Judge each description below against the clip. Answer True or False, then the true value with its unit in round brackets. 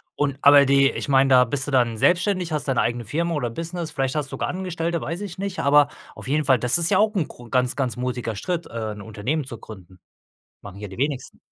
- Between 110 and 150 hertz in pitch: True (140 Hz)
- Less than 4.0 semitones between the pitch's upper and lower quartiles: False (5.4 semitones)